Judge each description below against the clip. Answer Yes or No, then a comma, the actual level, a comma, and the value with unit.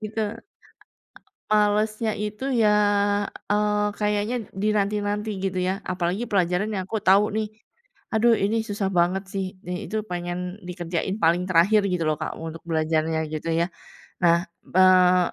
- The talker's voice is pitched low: No, high, 195 Hz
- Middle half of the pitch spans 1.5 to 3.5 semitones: Yes, average, 2.8 semitones